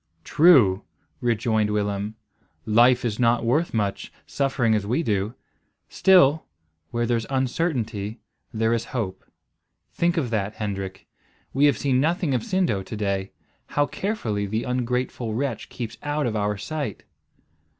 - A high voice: No, low, 115 Hz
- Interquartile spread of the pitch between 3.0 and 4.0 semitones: No, average, 4.6 semitones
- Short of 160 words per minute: Yes, average, 140 wpm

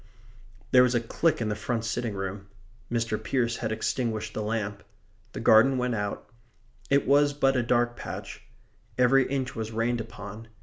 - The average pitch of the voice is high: No, low, 115 Hz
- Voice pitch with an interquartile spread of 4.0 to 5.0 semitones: No, narrow, 2.5 semitones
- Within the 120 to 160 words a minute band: No, average, 170 wpm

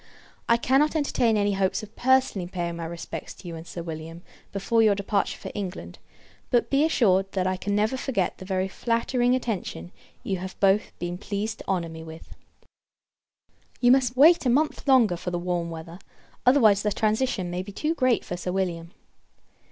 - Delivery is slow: No, average, 185 wpm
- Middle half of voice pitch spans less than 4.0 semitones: No, wide, 5.4 semitones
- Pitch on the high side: Yes, high, 195 Hz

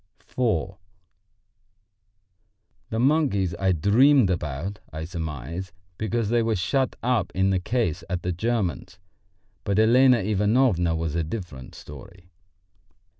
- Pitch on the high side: No, very low, 95 Hz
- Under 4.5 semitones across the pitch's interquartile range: No, wide, 5.4 semitones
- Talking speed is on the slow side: Yes, slow, 120 wpm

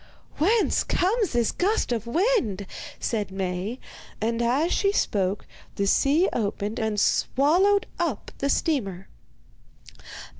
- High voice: Yes, high, 240 Hz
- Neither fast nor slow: No, slow, 115 wpm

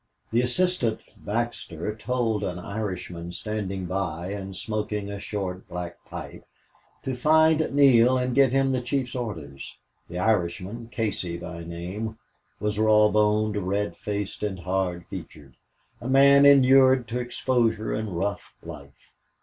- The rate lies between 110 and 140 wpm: Yes, slow, 135 wpm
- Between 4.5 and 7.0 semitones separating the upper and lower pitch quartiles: Yes, average, 5.0 semitones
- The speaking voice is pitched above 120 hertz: No, low, 105 Hz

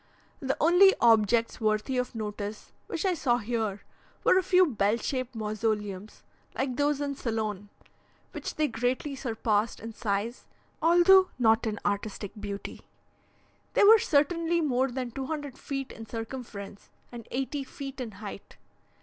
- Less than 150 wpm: Yes, average, 140 wpm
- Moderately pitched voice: No, high, 240 Hz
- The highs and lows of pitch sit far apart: No, average, 4.7 semitones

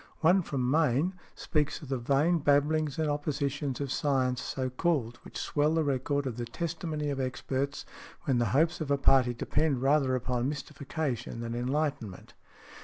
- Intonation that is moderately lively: Yes, average, 3.0 semitones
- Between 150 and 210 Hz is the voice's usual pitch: No, medium, 140 Hz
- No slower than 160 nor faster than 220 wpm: Yes, average, 165 wpm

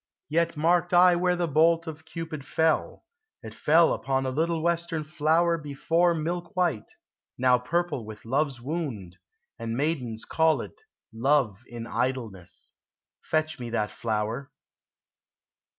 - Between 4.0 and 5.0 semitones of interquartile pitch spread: No, wide, 5.5 semitones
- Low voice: No, medium, 150 Hz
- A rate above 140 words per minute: No, slow, 135 wpm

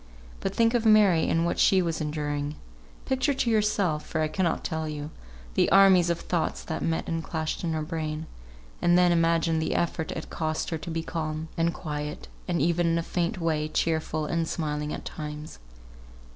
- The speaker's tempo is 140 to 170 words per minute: No, average, 190 wpm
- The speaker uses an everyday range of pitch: No, narrow, 1.9 semitones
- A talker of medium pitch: Yes, medium, 165 Hz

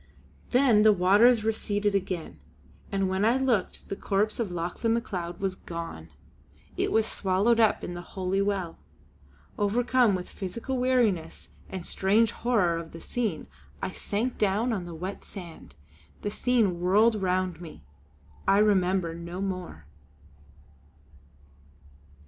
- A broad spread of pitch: No, average, 3.8 semitones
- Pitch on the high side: Yes, high, 195 Hz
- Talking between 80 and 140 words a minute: Yes, slow, 135 wpm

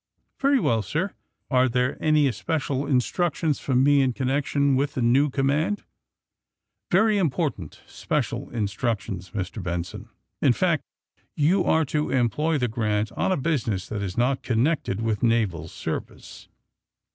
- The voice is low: Yes, low, 130 Hz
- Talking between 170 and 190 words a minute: No, average, 150 wpm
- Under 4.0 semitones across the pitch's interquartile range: No, average, 5.2 semitones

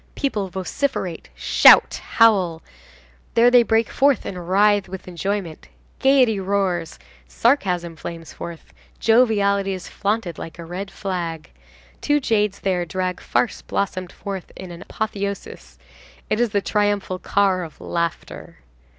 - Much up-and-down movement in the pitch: No, average, 3.3 semitones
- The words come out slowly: Yes, slow, 130 wpm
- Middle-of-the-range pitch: No, high, 195 Hz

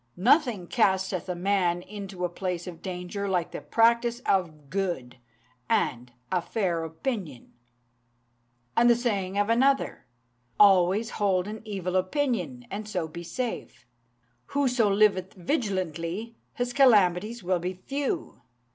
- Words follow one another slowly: Yes, slow, 130 wpm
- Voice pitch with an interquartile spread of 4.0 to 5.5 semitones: Yes, average, 4.3 semitones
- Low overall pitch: No, high, 190 Hz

